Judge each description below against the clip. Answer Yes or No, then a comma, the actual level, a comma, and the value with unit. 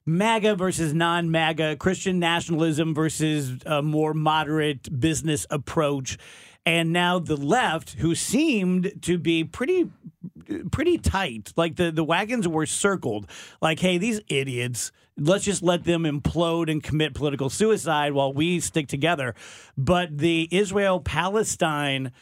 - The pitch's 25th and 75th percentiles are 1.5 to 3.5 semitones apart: Yes, average, 3.0 semitones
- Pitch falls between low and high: Yes, medium, 165 Hz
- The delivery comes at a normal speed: No, slow, 130 wpm